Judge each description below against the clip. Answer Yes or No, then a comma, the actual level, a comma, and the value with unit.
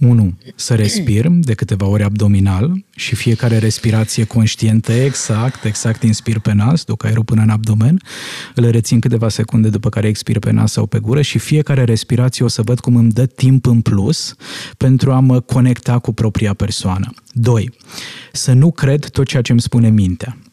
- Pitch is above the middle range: No, low, 115 Hz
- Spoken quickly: Yes, fast, 180 wpm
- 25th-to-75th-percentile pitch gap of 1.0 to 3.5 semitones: Yes, narrow, 2.6 semitones